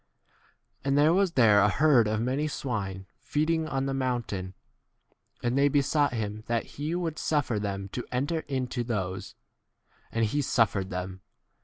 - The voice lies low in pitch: Yes, low, 125 Hz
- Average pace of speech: Yes, average, 160 wpm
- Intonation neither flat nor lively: No, wide, 5.7 semitones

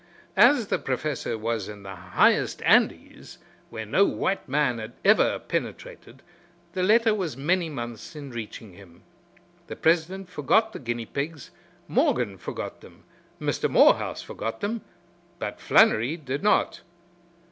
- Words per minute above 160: No, slow, 135 wpm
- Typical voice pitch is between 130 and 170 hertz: Yes, medium, 140 Hz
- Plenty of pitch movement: Yes, wide, 8.6 semitones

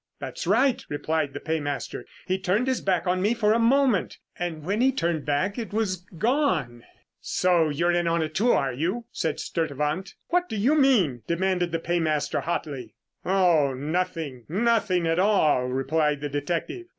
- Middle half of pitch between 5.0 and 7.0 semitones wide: Yes, wide, 5.6 semitones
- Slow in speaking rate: No, average, 170 wpm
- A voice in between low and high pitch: Yes, medium, 175 Hz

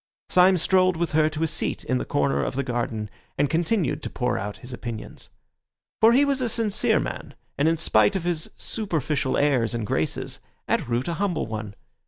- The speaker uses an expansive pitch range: Yes, wide, 7.4 semitones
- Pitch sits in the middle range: Yes, medium, 150 Hz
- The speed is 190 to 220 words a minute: Yes, average, 200 wpm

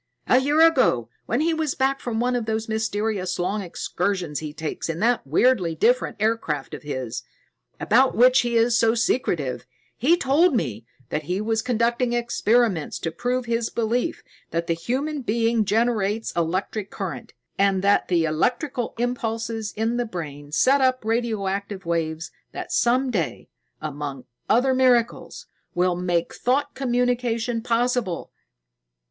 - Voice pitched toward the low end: No, high, 225 Hz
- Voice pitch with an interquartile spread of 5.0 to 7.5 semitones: Yes, wide, 5.6 semitones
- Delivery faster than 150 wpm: No, average, 145 wpm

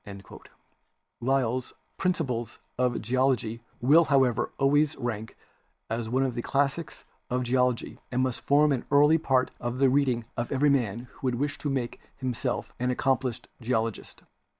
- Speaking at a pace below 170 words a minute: Yes, average, 150 wpm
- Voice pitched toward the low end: Yes, low, 130 Hz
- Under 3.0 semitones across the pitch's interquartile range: Yes, narrow, 2.4 semitones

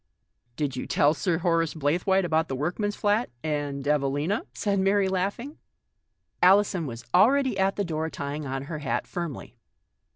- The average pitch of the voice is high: No, medium, 165 Hz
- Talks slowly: No, average, 160 wpm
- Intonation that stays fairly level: No, average, 5.2 semitones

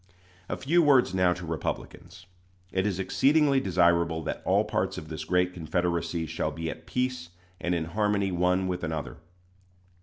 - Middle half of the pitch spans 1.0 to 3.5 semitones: Yes, average, 3.0 semitones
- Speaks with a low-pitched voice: Yes, very low, 90 Hz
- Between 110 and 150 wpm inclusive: No, average, 160 wpm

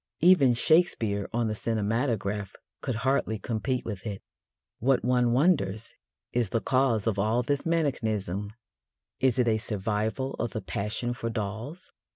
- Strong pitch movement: No, average, 3.5 semitones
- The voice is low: Yes, low, 115 Hz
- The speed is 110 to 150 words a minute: Yes, average, 145 wpm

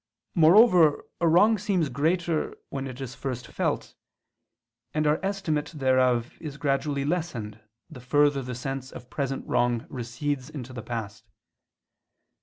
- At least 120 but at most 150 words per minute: Yes, slow, 135 wpm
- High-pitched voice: No, medium, 140 Hz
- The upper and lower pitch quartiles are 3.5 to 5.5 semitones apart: Yes, average, 4.0 semitones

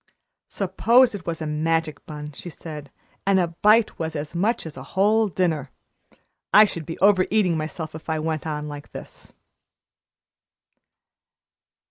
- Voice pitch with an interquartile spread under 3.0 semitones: No, average, 4.1 semitones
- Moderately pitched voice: Yes, medium, 165 Hz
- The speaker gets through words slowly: No, average, 150 wpm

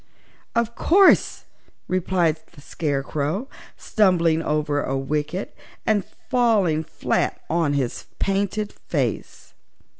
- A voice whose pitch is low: No, medium, 170 Hz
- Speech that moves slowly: Yes, slow, 95 wpm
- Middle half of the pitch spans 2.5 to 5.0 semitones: No, wide, 5.5 semitones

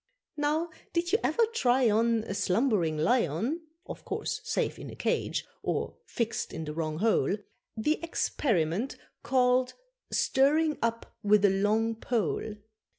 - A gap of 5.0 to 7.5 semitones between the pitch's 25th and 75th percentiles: Yes, wide, 5.4 semitones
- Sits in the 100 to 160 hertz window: No, high, 230 Hz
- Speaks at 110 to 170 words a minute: Yes, average, 140 wpm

